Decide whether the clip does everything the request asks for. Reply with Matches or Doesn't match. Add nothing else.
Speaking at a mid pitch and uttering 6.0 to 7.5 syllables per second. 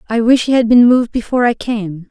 Doesn't match